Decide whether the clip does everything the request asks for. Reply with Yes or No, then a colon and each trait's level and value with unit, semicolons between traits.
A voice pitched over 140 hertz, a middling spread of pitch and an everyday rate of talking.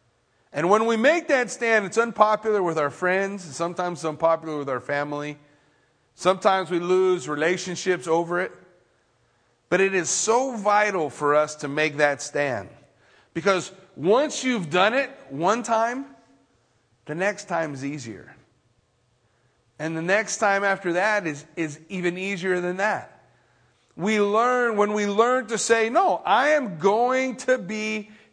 No: medium, 185 Hz; wide, 6.0 semitones; average, 150 wpm